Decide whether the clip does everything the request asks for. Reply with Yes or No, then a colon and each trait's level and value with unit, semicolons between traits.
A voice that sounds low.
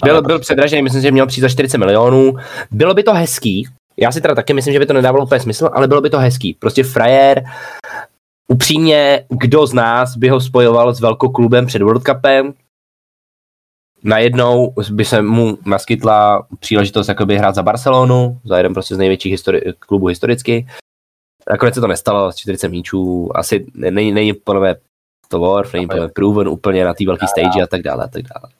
Yes: low, 115 Hz